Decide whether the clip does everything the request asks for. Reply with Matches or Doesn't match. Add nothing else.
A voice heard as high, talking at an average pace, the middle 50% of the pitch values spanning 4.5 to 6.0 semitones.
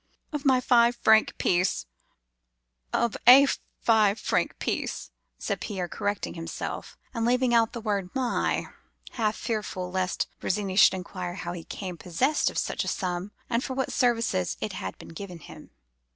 Matches